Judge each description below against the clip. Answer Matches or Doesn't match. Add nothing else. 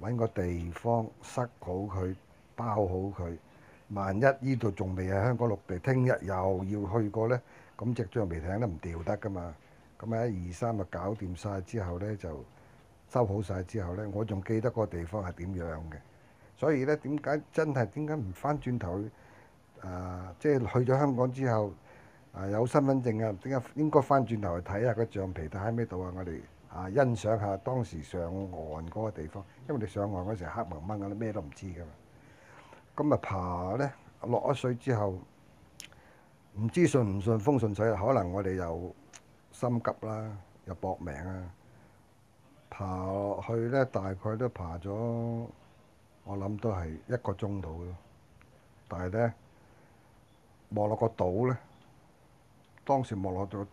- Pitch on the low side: Matches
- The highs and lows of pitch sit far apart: Doesn't match